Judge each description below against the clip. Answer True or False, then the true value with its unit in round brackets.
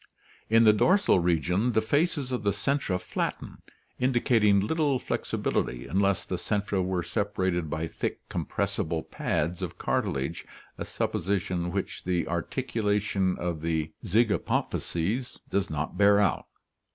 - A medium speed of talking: False (130 wpm)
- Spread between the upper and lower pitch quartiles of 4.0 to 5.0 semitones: True (4.3 semitones)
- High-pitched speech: False (95 Hz)